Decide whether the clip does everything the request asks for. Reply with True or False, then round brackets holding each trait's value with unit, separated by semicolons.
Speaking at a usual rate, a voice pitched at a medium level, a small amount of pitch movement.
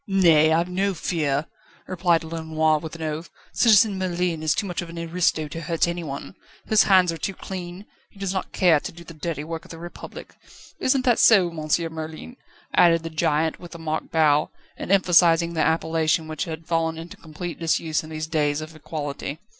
True (195 wpm; 165 Hz; 1.9 semitones)